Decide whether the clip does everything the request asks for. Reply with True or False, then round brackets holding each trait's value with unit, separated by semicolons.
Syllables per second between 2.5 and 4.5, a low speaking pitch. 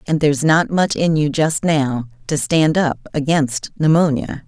False (4.2 syllables/s; 150 Hz)